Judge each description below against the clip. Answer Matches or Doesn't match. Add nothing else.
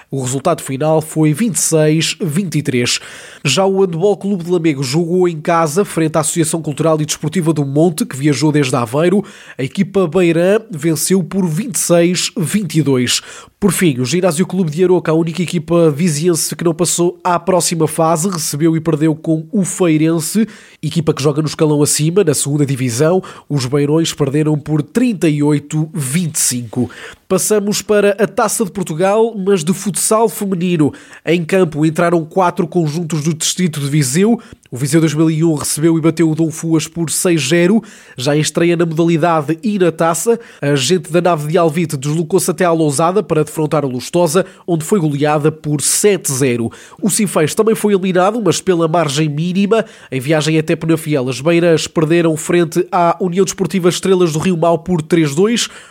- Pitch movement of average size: Matches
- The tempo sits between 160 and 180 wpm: Matches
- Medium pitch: Matches